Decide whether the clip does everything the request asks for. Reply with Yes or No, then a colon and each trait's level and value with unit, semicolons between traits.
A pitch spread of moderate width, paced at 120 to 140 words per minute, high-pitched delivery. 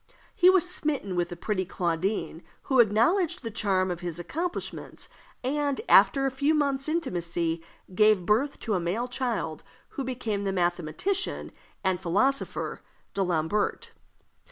No: wide, 7.6 semitones; slow, 135 wpm; high, 210 Hz